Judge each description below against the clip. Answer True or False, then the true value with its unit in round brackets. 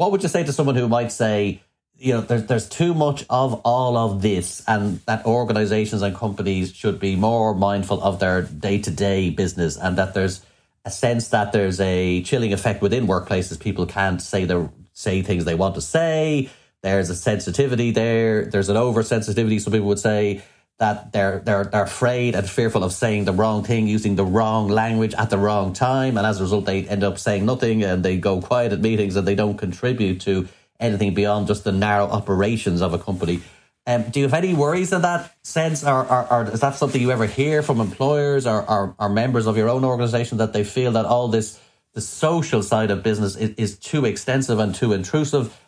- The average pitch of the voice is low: True (110 Hz)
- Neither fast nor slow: False (210 wpm)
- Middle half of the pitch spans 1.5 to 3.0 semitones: False (3.5 semitones)